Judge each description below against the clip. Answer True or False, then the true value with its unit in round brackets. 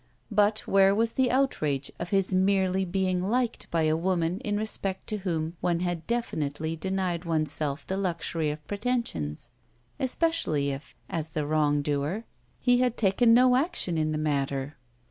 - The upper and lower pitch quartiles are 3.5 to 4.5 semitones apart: False (5.1 semitones)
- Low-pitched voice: False (180 Hz)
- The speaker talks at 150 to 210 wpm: True (165 wpm)